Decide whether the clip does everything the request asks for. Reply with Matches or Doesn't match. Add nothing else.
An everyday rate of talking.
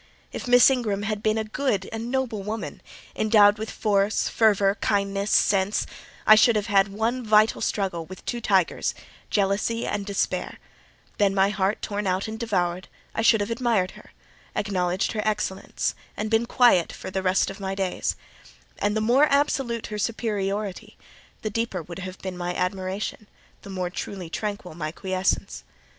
Matches